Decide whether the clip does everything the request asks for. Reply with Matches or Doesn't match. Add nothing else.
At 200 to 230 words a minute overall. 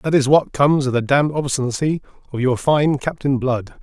Matches